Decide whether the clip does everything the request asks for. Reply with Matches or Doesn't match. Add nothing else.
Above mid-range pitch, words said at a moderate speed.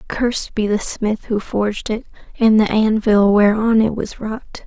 Matches